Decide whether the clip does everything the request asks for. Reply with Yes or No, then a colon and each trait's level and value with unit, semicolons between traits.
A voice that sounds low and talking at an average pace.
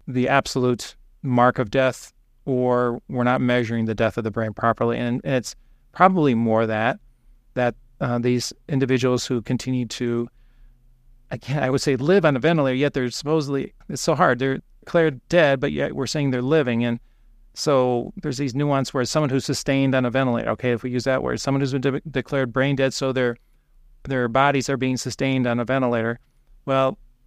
Yes: low, 130 Hz; average, 190 wpm